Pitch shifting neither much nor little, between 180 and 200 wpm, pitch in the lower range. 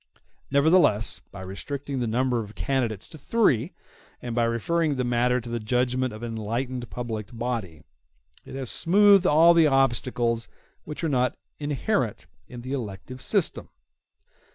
No: average, 3.5 semitones; average, 155 wpm; low, 125 Hz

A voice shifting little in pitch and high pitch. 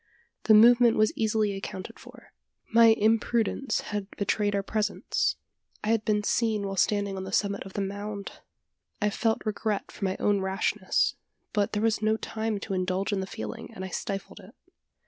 Yes: narrow, 1.9 semitones; high, 210 Hz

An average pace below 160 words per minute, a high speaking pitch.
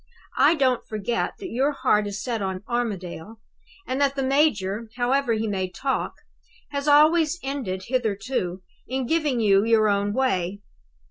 Yes: average, 150 wpm; high, 235 Hz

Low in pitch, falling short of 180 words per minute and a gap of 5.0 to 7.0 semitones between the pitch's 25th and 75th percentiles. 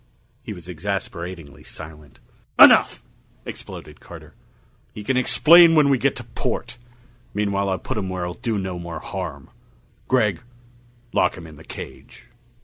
Yes: very low, 95 Hz; average, 145 wpm; average, 5.3 semitones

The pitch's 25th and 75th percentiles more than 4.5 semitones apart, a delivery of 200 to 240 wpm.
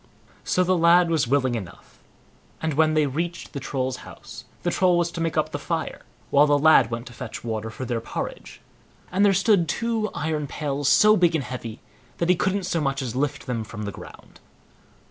Yes: average, 5.2 semitones; fast, 205 wpm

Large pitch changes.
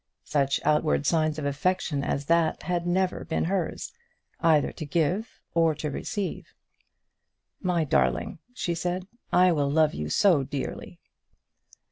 No: average, 3.7 semitones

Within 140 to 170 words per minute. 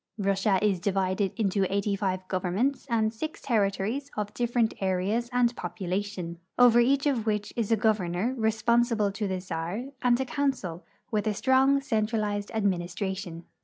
Yes: average, 155 wpm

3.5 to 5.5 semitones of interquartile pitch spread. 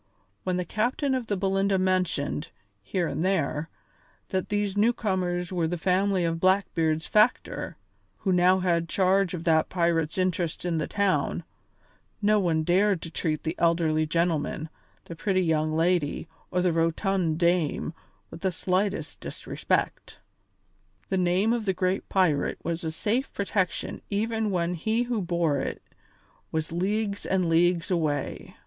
No: average, 2.9 semitones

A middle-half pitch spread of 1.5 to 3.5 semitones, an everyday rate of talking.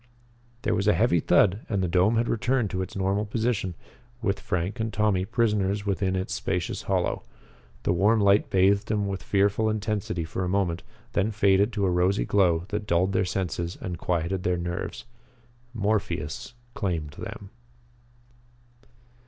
Yes: narrow, 2.6 semitones; average, 160 wpm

